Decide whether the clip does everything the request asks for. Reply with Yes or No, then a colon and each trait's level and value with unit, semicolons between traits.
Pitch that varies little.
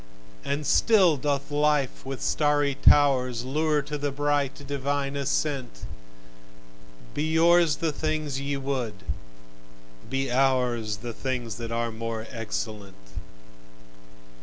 No: average, 3.0 semitones